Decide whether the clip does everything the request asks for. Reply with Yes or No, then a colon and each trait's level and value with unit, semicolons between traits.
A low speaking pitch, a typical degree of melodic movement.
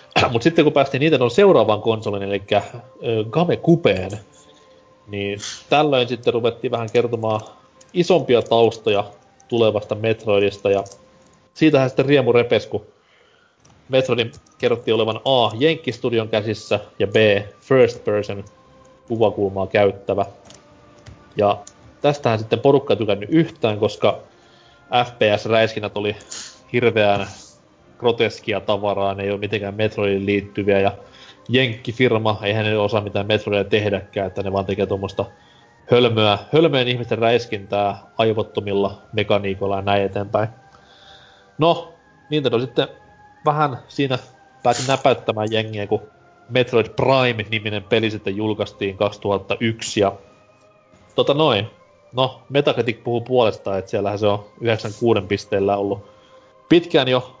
Yes: low, 110 Hz; average, 3.6 semitones